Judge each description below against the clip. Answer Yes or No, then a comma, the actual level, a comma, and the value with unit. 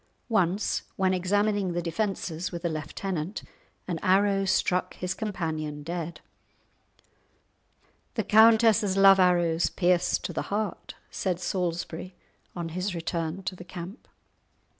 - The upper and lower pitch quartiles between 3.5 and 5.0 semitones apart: No, narrow, 2.5 semitones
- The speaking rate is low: Yes, slow, 120 wpm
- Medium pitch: Yes, medium, 180 Hz